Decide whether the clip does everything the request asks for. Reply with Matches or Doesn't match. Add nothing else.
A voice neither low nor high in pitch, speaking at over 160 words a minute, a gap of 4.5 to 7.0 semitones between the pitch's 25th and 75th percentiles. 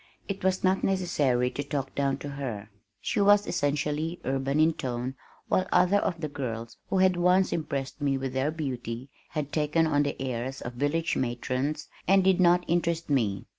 Matches